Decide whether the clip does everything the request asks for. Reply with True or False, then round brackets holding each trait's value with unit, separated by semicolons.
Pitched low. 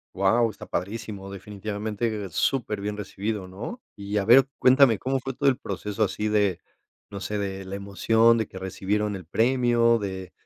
True (105 Hz)